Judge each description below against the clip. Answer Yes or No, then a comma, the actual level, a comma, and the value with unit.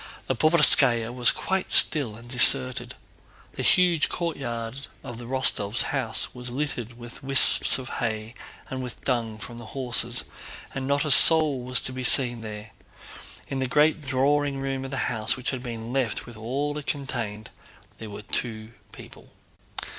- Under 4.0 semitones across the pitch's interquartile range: Yes, average, 2.9 semitones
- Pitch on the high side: No, low, 125 Hz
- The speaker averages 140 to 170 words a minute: Yes, average, 160 wpm